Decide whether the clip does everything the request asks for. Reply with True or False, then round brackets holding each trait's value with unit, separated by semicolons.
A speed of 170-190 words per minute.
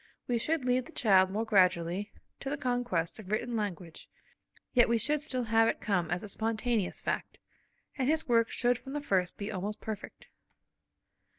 True (180 wpm)